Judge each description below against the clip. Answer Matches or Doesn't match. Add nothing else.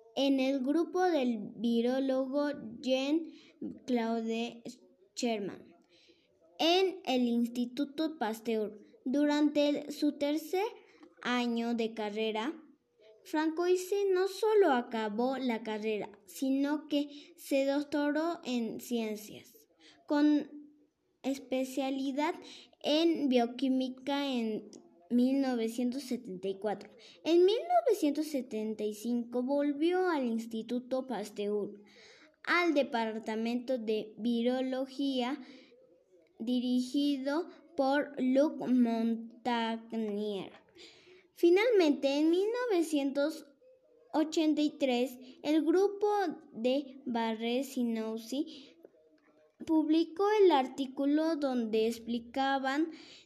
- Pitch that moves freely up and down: Doesn't match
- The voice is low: Doesn't match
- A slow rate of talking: Matches